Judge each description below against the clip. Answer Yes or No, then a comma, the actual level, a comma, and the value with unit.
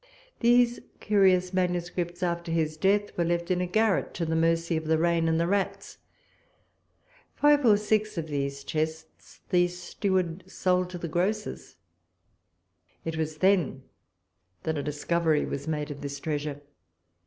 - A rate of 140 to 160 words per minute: Yes, average, 150 wpm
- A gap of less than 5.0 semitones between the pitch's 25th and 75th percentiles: Yes, average, 2.9 semitones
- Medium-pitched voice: Yes, medium, 170 Hz